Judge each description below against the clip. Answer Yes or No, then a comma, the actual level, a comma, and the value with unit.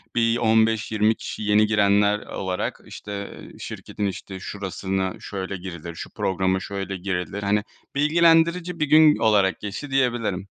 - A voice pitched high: No, low, 105 Hz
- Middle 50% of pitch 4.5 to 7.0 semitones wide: No, average, 3.3 semitones